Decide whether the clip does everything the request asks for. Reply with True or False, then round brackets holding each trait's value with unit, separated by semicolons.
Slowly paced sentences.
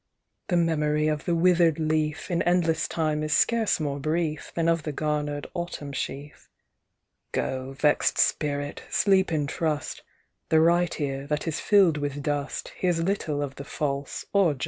False (165 wpm)